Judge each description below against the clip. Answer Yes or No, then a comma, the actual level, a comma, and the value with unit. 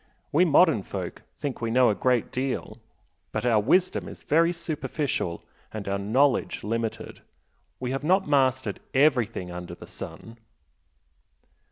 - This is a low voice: Yes, low, 130 Hz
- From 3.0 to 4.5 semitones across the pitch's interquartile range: No, average, 4.9 semitones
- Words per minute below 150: Yes, average, 140 wpm